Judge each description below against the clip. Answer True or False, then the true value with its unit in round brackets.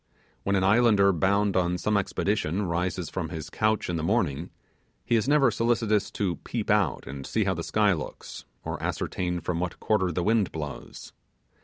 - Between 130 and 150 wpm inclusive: False (180 wpm)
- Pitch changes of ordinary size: True (3.6 semitones)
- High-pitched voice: False (95 Hz)